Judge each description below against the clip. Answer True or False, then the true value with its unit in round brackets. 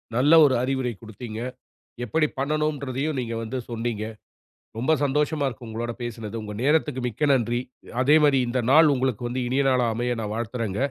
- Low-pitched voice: True (125 Hz)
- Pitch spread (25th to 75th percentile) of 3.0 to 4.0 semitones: True (3.4 semitones)